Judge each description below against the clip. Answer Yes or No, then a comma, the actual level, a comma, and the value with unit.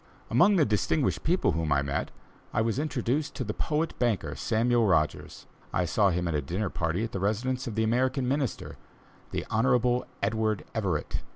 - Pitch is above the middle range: No, low, 110 Hz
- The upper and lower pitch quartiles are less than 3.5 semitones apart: No, average, 4.8 semitones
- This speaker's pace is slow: No, average, 180 wpm